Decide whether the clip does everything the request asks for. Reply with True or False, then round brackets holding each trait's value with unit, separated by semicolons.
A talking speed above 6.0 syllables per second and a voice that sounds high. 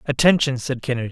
False (7.1 syllables/s; 135 Hz)